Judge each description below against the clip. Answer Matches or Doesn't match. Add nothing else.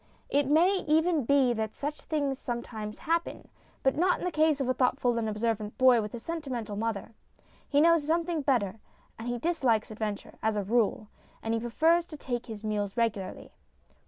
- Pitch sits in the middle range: Doesn't match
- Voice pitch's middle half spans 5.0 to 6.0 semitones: Matches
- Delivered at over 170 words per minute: Matches